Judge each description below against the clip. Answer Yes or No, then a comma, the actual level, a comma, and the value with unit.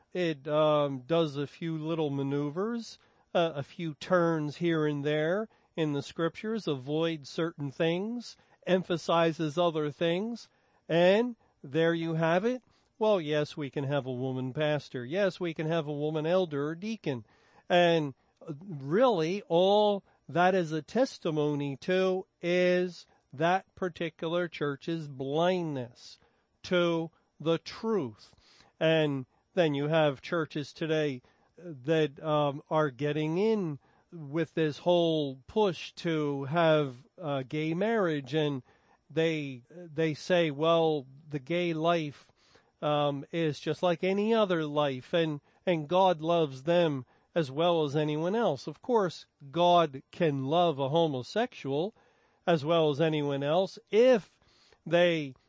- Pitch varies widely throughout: No, average, 2.9 semitones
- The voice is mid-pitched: Yes, medium, 165 Hz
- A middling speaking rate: No, slow, 130 wpm